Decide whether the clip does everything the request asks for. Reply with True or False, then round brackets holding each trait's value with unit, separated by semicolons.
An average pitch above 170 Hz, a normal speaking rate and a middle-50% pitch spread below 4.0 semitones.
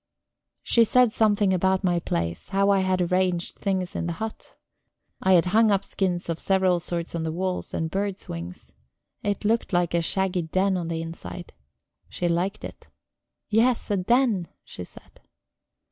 True (185 Hz; 170 wpm; 2.7 semitones)